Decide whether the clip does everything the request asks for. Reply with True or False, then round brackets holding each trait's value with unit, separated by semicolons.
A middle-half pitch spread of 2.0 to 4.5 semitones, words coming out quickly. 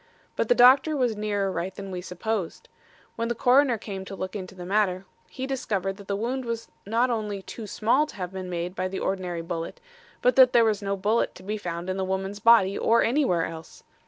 True (3.8 semitones; 220 wpm)